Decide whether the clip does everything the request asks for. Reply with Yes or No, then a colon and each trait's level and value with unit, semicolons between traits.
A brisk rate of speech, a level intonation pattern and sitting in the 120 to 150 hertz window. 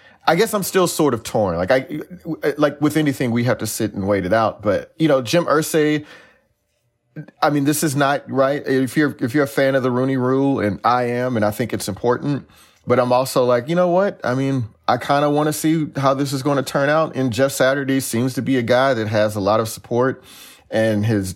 No: fast, 245 wpm; average, 3.8 semitones; low, 135 Hz